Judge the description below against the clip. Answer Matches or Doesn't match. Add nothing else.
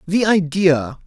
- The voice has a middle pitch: Matches